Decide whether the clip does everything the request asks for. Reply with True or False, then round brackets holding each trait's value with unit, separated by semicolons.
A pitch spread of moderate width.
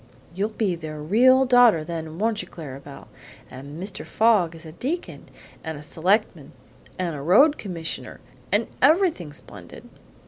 False (6.3 semitones)